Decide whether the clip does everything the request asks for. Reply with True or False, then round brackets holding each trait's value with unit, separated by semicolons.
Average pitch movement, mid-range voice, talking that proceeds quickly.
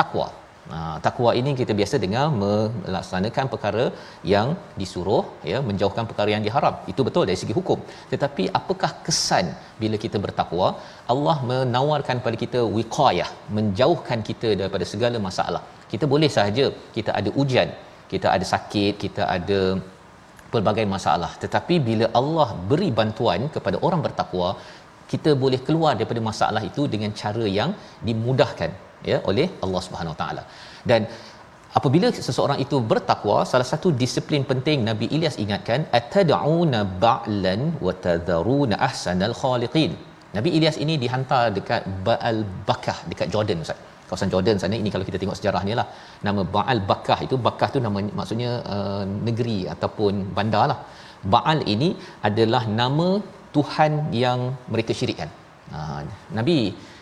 False (4.6 semitones; 115 Hz; 140 wpm)